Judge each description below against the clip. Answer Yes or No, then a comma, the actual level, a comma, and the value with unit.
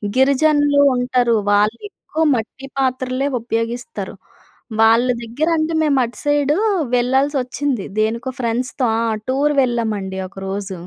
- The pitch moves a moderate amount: Yes, average, 3.5 semitones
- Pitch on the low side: No, very high, 250 Hz